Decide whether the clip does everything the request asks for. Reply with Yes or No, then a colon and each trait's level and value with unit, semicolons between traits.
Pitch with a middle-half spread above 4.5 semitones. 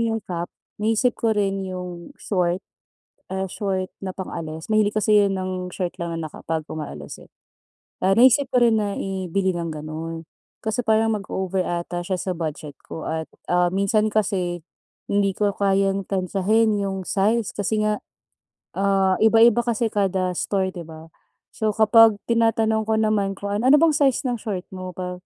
No: average, 3.2 semitones